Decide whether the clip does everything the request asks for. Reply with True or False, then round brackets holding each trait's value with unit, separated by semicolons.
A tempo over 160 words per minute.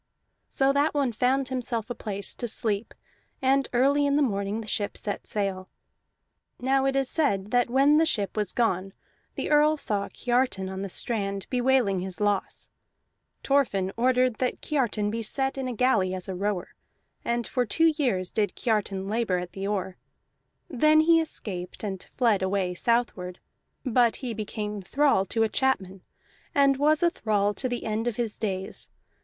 True (170 wpm)